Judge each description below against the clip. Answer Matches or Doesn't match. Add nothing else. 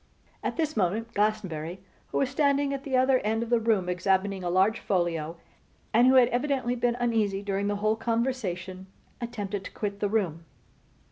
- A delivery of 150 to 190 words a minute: Matches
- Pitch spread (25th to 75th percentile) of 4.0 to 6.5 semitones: Matches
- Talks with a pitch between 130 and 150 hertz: Doesn't match